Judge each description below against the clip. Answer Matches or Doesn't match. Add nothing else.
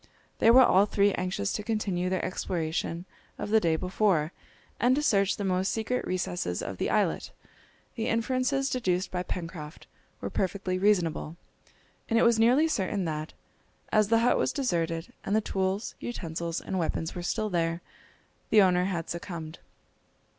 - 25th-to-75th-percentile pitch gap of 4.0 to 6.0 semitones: Matches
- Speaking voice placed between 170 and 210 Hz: Matches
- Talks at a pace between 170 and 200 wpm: Doesn't match